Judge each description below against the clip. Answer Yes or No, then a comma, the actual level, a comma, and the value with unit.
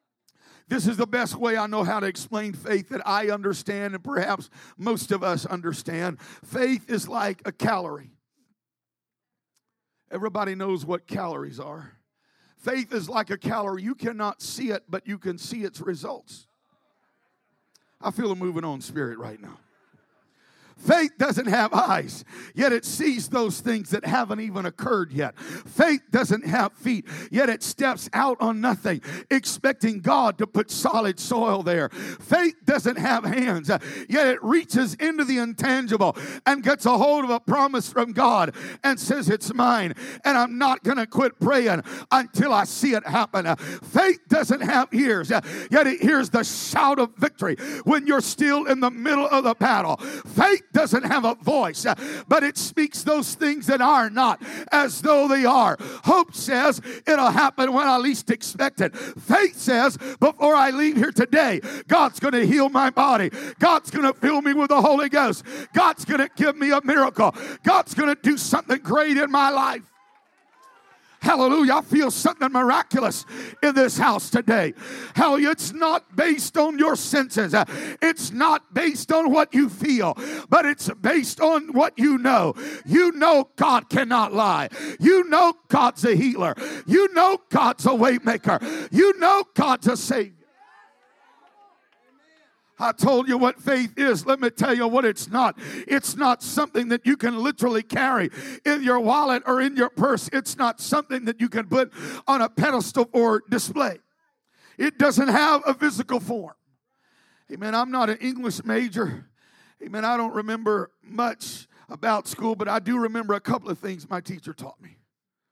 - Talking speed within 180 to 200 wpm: No, average, 165 wpm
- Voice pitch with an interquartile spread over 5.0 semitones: No, average, 4.3 semitones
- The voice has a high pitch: Yes, very high, 250 Hz